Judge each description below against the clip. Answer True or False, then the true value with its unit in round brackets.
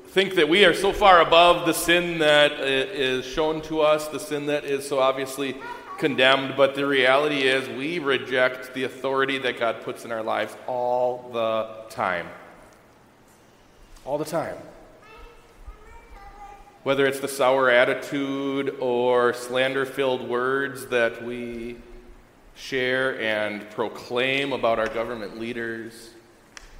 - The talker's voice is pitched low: True (130 Hz)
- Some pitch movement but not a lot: True (3.4 semitones)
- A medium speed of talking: False (130 wpm)